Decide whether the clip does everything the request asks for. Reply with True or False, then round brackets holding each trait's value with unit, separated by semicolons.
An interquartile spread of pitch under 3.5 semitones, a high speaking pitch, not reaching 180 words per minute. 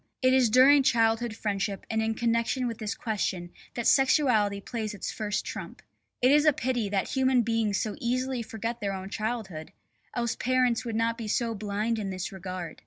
False (3.0 semitones; 225 Hz; 185 wpm)